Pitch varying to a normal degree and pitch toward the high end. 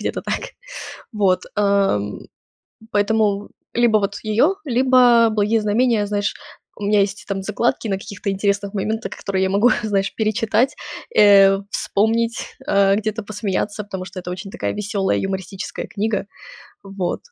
No: narrow, 2.0 semitones; high, 205 Hz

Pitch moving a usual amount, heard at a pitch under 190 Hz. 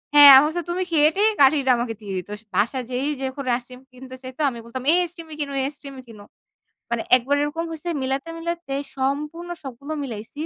No: average, 3.4 semitones; very high, 275 Hz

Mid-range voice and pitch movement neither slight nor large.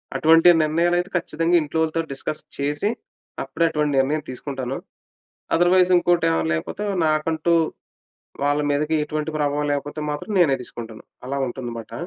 Yes: medium, 150 Hz; average, 3.2 semitones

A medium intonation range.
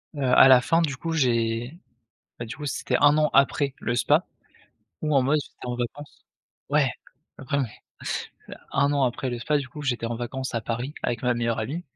Yes: average, 3.3 semitones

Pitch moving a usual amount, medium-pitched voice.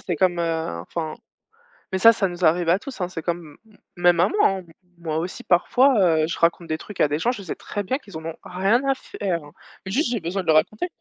Yes: average, 3.5 semitones; medium, 175 Hz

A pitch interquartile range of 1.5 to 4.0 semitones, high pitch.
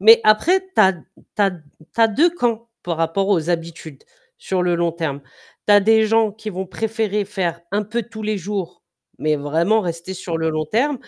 No: average, 4.6 semitones; high, 195 Hz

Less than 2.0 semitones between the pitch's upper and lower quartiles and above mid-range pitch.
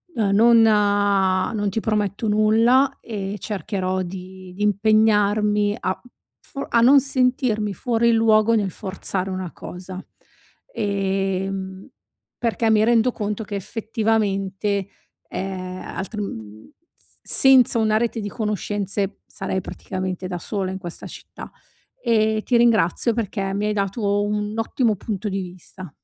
No: narrow, 2.6 semitones; high, 205 Hz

